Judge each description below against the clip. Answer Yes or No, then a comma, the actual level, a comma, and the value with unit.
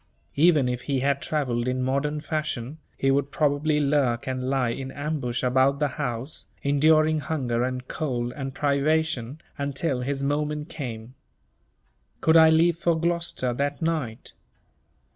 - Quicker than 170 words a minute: No, average, 145 wpm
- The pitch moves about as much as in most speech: Yes, average, 3.2 semitones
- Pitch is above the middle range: No, medium, 140 Hz